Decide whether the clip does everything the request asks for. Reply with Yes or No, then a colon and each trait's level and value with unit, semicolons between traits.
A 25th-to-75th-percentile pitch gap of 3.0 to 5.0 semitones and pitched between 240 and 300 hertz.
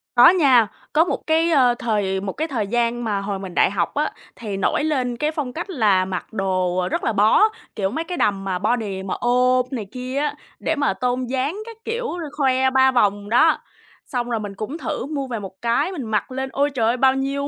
No: wide, 5.4 semitones; high, 245 Hz